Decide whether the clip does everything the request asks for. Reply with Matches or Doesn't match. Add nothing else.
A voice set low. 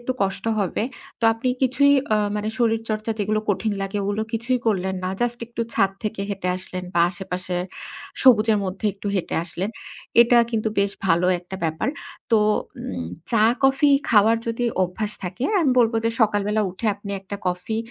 Doesn't match